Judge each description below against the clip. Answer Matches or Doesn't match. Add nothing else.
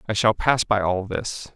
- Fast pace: Matches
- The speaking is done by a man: Matches